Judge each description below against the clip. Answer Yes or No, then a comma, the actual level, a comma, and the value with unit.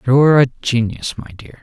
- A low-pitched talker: Yes, low, 125 Hz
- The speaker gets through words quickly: No, average, 185 wpm